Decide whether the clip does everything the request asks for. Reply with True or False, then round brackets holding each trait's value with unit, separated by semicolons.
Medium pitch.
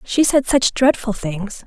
False (235 Hz)